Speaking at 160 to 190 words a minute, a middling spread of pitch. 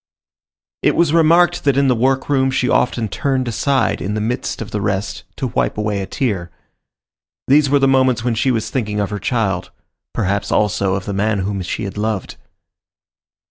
Yes: average, 185 wpm; average, 4.6 semitones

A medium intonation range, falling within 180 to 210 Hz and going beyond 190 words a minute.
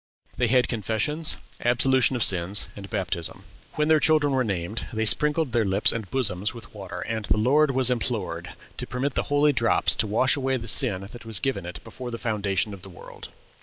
No: average, 4.8 semitones; low, 115 Hz; fast, 205 wpm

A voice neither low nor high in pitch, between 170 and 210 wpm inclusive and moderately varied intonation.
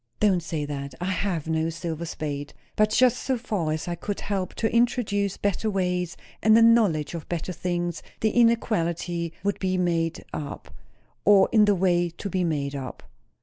Yes: medium, 180 Hz; average, 180 wpm; average, 3.9 semitones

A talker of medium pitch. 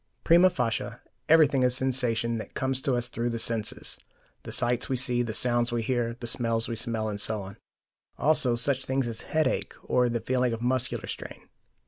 No: low, 120 Hz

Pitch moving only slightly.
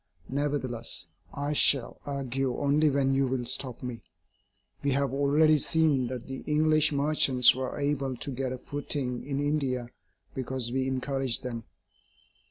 Yes: narrow, 2.0 semitones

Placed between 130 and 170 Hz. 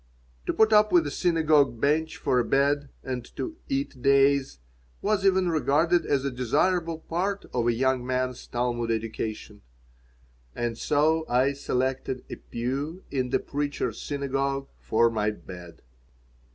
Yes: medium, 140 Hz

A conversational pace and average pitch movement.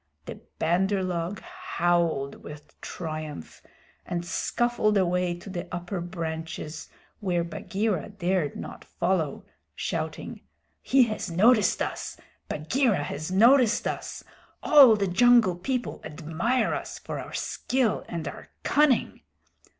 No: slow, 120 wpm; average, 5.0 semitones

